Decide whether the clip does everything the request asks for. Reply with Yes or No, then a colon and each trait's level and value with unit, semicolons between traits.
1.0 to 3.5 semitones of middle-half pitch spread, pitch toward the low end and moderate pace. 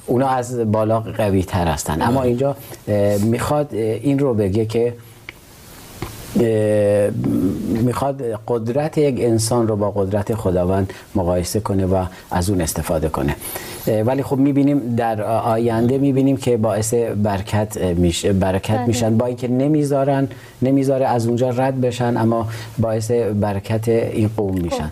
Yes: average, 3.2 semitones; low, 115 Hz; average, 130 wpm